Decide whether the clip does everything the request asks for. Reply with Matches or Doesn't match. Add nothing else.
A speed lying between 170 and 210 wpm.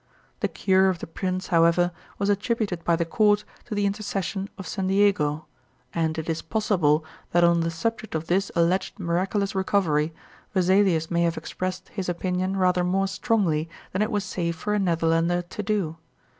Matches